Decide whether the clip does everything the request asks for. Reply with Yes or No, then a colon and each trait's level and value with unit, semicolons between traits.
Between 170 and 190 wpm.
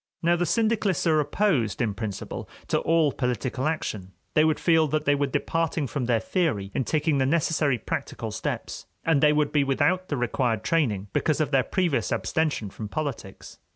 Yes: average, 185 wpm